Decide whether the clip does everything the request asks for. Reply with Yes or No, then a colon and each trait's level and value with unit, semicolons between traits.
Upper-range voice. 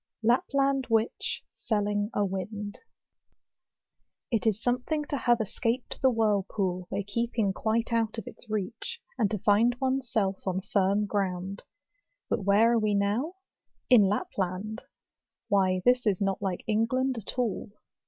Yes: high, 215 Hz